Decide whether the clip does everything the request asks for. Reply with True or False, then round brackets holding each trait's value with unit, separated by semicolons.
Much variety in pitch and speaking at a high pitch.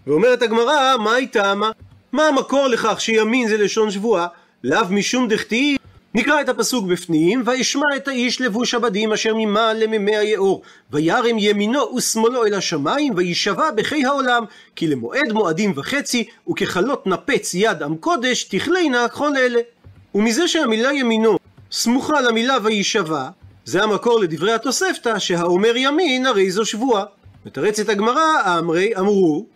False (4.0 semitones; 225 Hz)